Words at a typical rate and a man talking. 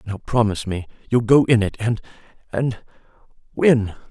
No: slow, 115 wpm; male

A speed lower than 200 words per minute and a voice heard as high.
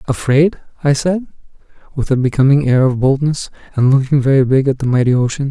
No: average, 185 wpm; low, 135 Hz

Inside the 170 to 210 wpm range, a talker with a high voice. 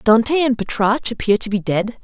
Yes: fast, 205 wpm; high, 230 Hz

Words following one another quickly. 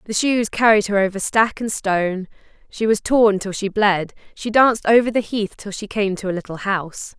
Yes: fast, 215 wpm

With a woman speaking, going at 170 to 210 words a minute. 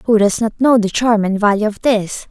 No: female; fast, 260 wpm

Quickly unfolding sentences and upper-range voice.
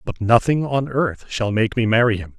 No: fast, 225 wpm; low, 115 Hz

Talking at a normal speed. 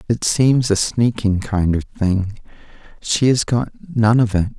Yes: average, 170 wpm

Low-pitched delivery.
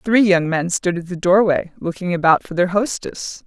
No: medium, 185 Hz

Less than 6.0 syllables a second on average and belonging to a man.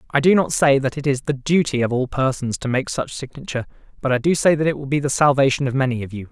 No: 6.6 syllables/s; male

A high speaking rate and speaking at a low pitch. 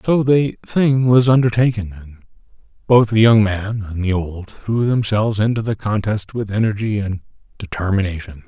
No: average, 155 wpm; low, 105 Hz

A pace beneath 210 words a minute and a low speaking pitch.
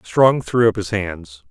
Yes: average, 200 wpm; low, 100 Hz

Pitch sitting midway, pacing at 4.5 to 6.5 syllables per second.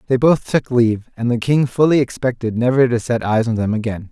No: low, 120 Hz; 5.7 syllables/s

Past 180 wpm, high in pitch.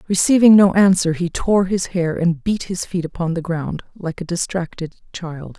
No: average, 195 wpm; medium, 175 Hz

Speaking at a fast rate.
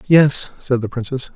No: average, 175 wpm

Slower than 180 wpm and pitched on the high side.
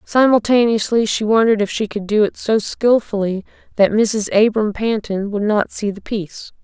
Yes: average, 170 wpm; high, 215 Hz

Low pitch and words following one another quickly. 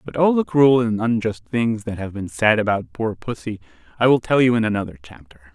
Yes: low, 115 Hz; fast, 225 wpm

